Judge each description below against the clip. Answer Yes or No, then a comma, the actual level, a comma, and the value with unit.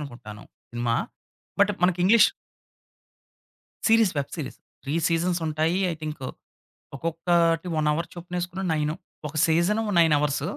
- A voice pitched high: No, medium, 165 Hz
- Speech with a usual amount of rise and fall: Yes, average, 3.0 semitones